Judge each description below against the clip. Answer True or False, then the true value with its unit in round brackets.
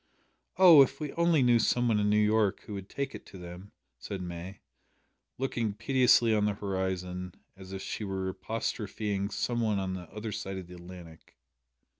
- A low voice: True (100 Hz)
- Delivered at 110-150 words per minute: False (185 wpm)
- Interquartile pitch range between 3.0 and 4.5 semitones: True (3.5 semitones)